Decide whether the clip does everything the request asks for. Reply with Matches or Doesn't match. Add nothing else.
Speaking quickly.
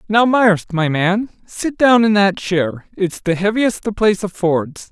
Doesn't match